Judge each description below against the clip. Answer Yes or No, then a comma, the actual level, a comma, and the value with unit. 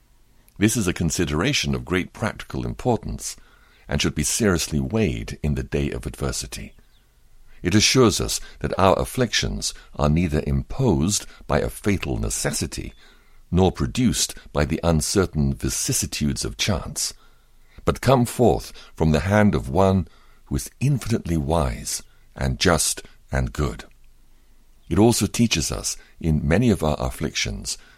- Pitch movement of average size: No, wide, 6.2 semitones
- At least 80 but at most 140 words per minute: Yes, slow, 135 wpm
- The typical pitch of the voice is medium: No, very low, 80 Hz